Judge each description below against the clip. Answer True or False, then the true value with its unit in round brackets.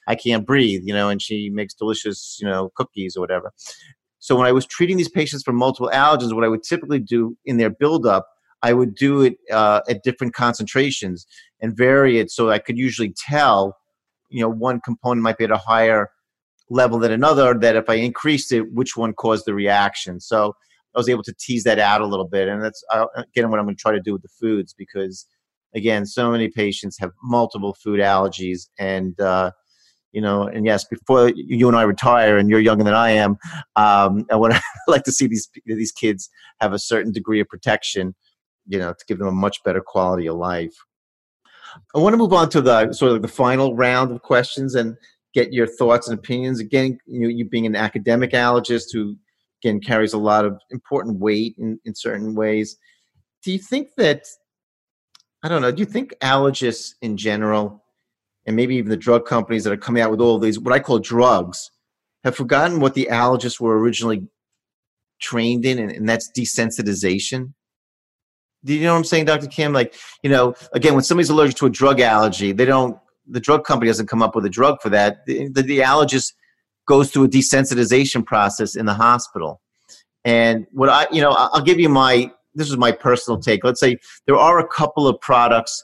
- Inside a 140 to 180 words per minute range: False (205 wpm)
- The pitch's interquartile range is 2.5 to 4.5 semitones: True (3.3 semitones)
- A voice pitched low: True (115 Hz)